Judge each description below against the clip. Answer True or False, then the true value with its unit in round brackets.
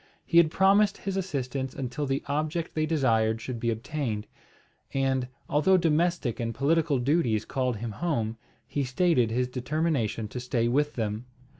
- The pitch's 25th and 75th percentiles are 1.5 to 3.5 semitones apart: False (5.0 semitones)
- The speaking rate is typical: True (155 wpm)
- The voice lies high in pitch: False (135 Hz)